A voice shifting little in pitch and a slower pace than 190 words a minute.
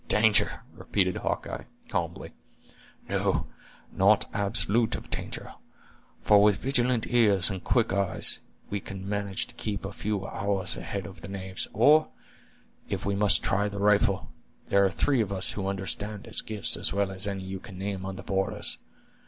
Yes: narrow, 1.6 semitones; average, 170 wpm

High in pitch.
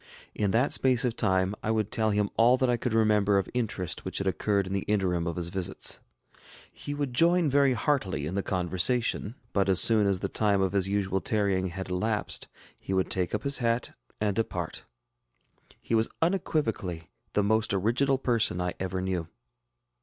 No: low, 105 Hz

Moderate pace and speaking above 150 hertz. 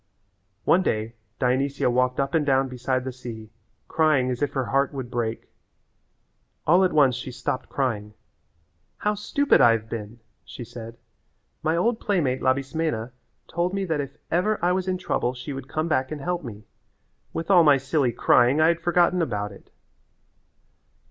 No: average, 170 wpm; low, 135 Hz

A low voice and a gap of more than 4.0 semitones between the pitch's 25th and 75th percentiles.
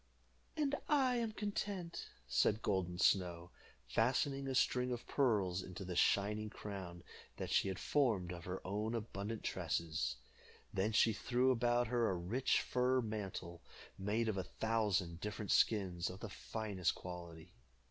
Yes: low, 105 Hz; average, 5.1 semitones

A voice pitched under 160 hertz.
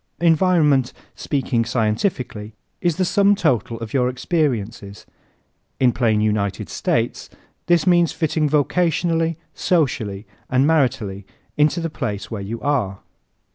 Yes: low, 135 Hz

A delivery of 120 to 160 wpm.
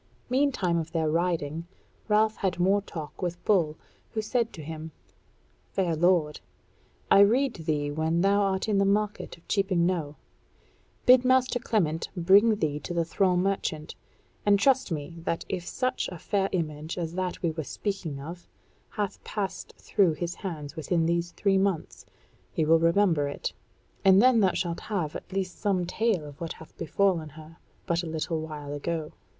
No: average, 170 wpm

